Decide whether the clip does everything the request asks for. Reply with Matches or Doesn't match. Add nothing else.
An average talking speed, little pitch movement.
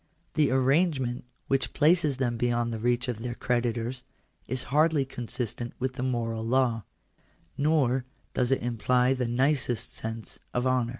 Matches